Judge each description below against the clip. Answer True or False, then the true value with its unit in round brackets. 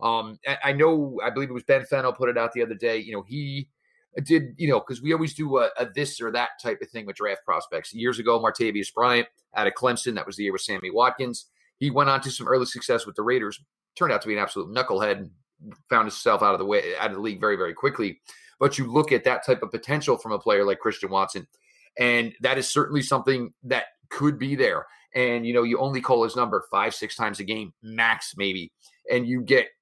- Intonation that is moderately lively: True (3.5 semitones)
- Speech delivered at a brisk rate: True (245 wpm)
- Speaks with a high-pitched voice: False (125 Hz)